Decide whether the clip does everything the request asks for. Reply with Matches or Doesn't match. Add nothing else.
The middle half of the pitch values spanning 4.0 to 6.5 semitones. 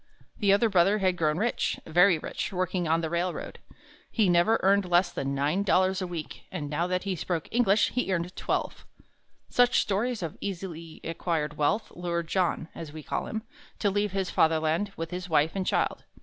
Doesn't match